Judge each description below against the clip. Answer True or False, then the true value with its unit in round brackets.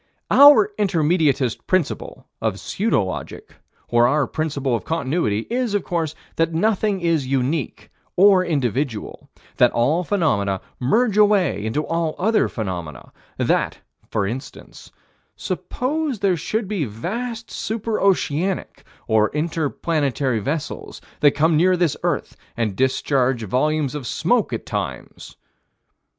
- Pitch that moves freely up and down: True (7.0 semitones)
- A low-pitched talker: False (155 Hz)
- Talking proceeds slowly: True (130 wpm)